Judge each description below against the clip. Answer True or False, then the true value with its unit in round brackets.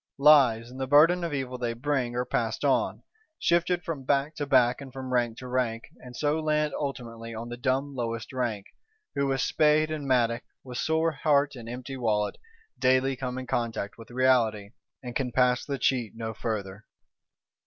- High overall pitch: False (130 Hz)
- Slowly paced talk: False (185 wpm)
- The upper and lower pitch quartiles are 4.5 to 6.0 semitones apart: False (3.1 semitones)